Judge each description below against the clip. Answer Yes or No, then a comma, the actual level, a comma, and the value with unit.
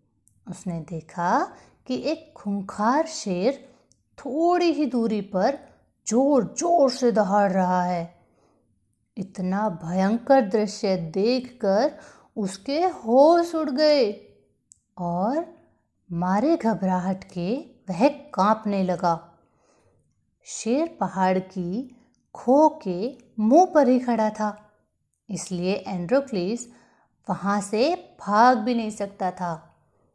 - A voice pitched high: Yes, high, 215 Hz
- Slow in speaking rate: Yes, slow, 100 wpm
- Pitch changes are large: Yes, wide, 6.3 semitones